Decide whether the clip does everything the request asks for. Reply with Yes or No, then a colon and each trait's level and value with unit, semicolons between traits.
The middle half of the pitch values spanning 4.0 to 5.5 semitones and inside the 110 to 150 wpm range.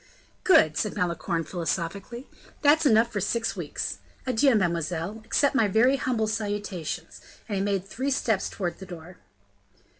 Yes: average, 4.9 semitones; average, 145 wpm